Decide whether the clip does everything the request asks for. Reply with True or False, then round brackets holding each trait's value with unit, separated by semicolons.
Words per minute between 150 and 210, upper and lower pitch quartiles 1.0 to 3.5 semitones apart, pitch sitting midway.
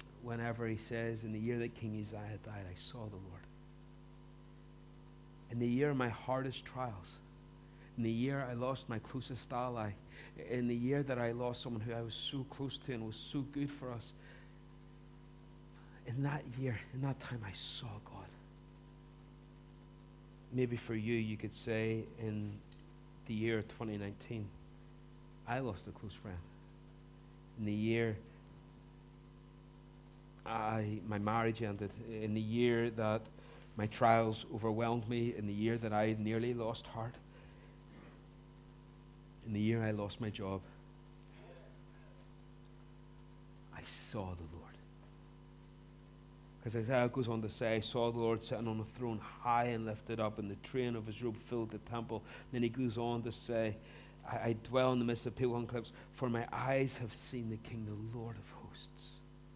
False (160 wpm; 2.5 semitones; 115 Hz)